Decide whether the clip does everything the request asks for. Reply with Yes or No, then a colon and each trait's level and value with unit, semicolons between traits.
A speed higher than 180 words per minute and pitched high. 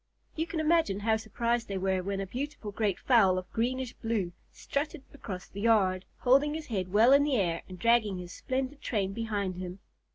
Yes: average, 195 wpm; high, 220 Hz